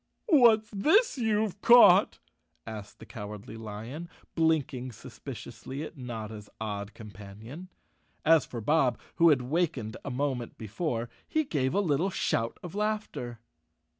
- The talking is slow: Yes, slow, 130 wpm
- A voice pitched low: Yes, low, 130 Hz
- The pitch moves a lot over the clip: Yes, wide, 8.0 semitones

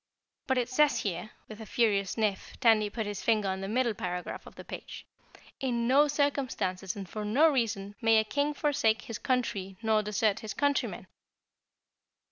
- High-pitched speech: Yes, high, 220 Hz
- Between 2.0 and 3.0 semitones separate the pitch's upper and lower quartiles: No, average, 4.1 semitones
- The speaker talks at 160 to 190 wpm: Yes, average, 175 wpm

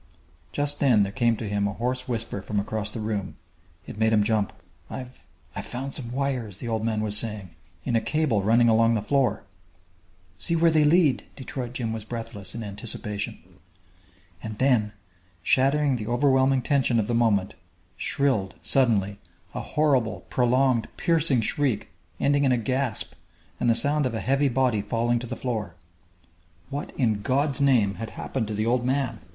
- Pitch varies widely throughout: No, average, 3.9 semitones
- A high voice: No, low, 120 Hz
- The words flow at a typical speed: Yes, average, 175 wpm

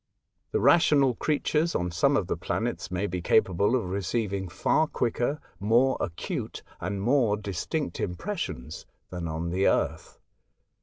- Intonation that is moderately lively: No, wide, 6.9 semitones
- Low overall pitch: Yes, low, 100 Hz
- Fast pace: No, average, 145 wpm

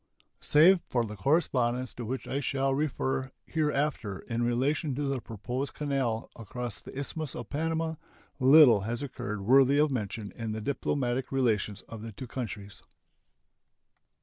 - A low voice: Yes, low, 130 Hz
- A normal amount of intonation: Yes, average, 3.7 semitones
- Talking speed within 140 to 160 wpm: Yes, average, 150 wpm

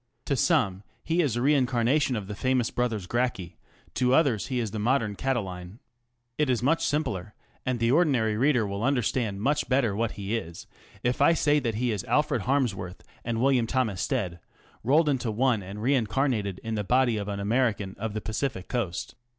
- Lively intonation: No, average, 4.2 semitones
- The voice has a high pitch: No, low, 120 Hz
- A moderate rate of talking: Yes, average, 185 wpm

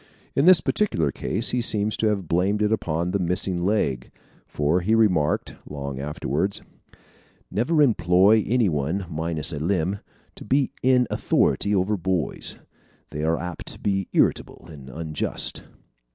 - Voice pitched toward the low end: Yes, very low, 90 Hz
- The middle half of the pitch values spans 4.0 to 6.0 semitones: Yes, average, 5.1 semitones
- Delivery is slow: No, average, 150 wpm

